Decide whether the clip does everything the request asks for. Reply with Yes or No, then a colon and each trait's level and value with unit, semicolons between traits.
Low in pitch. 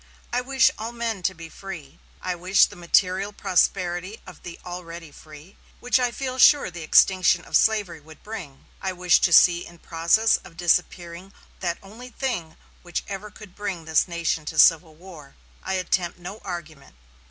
No: medium, 180 Hz